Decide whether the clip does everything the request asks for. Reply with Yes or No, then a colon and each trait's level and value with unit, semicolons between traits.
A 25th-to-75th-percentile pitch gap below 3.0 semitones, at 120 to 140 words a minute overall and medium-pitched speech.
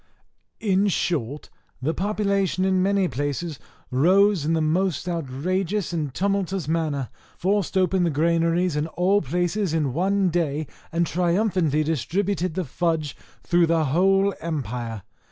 No: average, 3.8 semitones; slow, 135 wpm; medium, 170 Hz